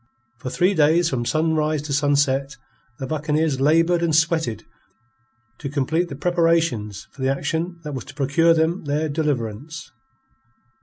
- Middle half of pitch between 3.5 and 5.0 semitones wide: No, average, 3.1 semitones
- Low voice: No, medium, 150 Hz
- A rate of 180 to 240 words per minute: No, average, 145 wpm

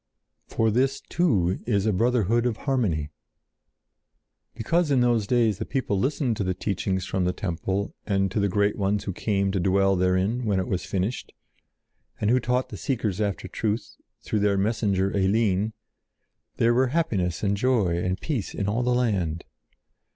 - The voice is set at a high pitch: No, low, 105 Hz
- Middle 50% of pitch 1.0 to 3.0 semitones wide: No, average, 3.9 semitones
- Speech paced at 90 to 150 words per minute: No, average, 170 wpm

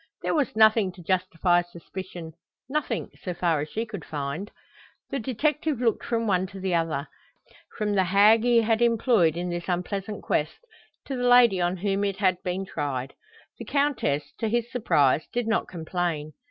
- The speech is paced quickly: No, average, 175 wpm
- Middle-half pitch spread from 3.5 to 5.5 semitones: Yes, average, 4.8 semitones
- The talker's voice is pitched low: No, high, 195 Hz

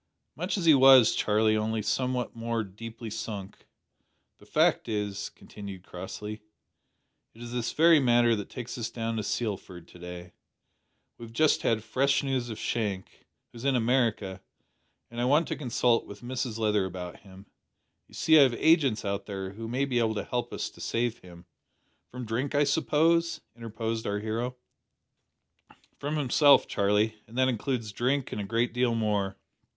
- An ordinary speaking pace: Yes, average, 175 wpm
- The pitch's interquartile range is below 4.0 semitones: Yes, average, 3.5 semitones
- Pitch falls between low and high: No, low, 115 Hz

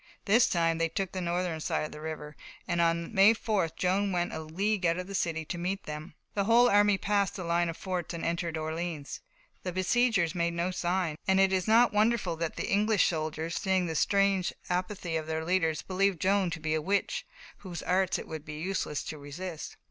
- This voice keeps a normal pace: No, fast, 215 wpm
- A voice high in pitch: No, medium, 175 Hz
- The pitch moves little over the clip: No, average, 3.1 semitones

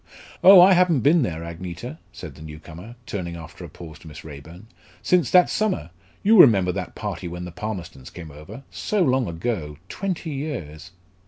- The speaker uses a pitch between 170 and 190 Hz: No, very low, 90 Hz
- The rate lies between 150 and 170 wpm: No, average, 180 wpm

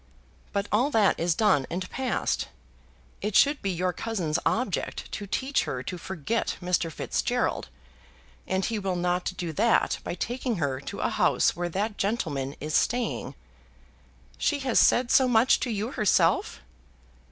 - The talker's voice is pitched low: No, high, 200 Hz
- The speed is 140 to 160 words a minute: Yes, average, 155 wpm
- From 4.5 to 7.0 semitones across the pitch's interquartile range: Yes, average, 4.9 semitones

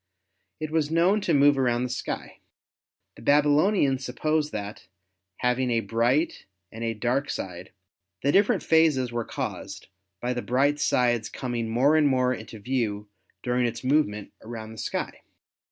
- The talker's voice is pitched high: No, low, 125 Hz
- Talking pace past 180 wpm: No, average, 155 wpm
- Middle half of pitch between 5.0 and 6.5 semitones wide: No, average, 4.0 semitones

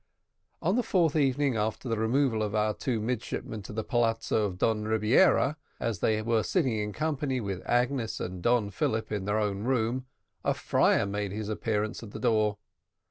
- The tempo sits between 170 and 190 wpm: Yes, average, 185 wpm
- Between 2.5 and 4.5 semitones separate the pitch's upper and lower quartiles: Yes, average, 3.2 semitones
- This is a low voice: Yes, low, 110 Hz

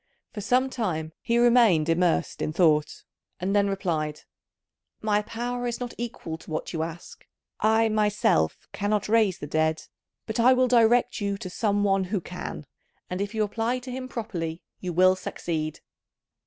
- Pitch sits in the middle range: No, high, 205 Hz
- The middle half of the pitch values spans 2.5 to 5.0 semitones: No, wide, 5.5 semitones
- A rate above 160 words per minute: Yes, average, 170 wpm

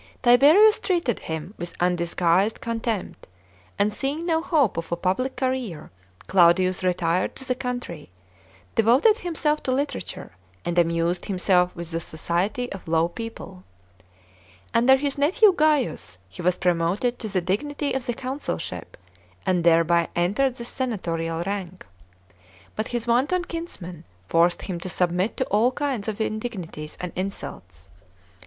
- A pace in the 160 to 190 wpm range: No, average, 140 wpm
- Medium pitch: No, high, 200 Hz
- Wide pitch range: Yes, wide, 7.0 semitones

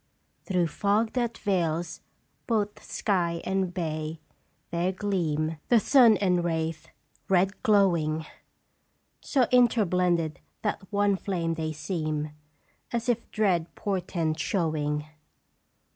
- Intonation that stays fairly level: No, average, 4.1 semitones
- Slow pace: Yes, slow, 105 wpm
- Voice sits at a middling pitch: Yes, medium, 180 Hz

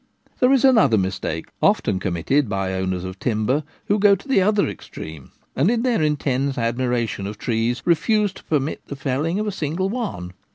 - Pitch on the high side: No, low, 135 Hz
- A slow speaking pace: No, average, 180 wpm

